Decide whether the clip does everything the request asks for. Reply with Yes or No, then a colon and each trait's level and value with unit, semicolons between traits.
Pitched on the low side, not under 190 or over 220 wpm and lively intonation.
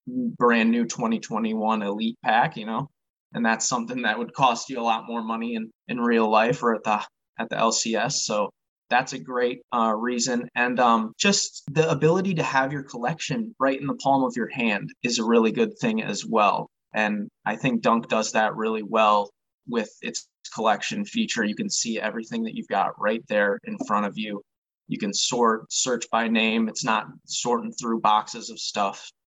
Yes: low, 120 Hz; average, 195 wpm; wide, 6.4 semitones